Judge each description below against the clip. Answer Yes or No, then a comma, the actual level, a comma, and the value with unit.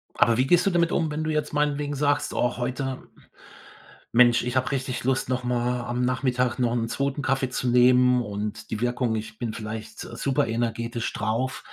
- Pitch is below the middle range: Yes, low, 125 Hz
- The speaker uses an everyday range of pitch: No, narrow, 2.3 semitones